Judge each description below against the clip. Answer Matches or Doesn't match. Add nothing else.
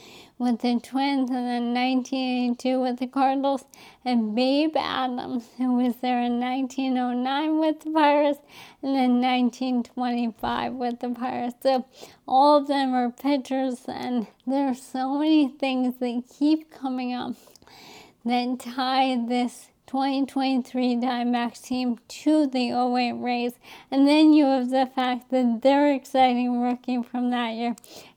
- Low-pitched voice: Doesn't match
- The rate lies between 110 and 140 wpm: Matches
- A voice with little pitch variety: Matches